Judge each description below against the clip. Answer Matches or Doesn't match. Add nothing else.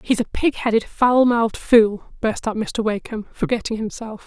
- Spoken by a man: Doesn't match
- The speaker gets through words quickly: Doesn't match